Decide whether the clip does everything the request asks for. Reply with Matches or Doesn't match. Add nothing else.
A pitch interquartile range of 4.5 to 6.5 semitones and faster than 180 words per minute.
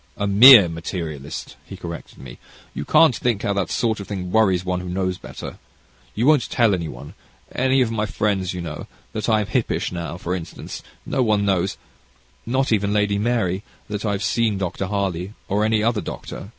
Doesn't match